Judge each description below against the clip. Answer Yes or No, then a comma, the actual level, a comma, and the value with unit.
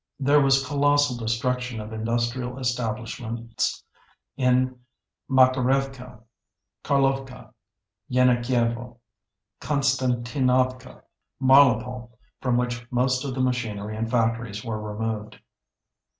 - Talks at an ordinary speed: No, slow, 85 wpm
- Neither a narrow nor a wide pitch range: No, narrow, 2.2 semitones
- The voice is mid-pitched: No, low, 125 Hz